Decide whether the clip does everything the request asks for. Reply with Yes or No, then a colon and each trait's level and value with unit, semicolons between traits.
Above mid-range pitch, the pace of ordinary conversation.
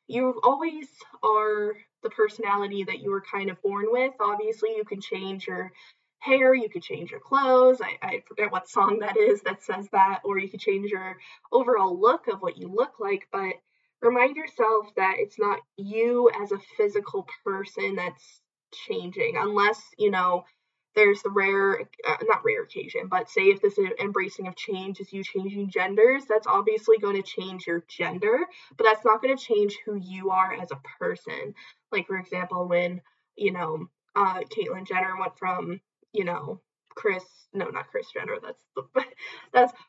Yes: high, 220 Hz; average, 180 wpm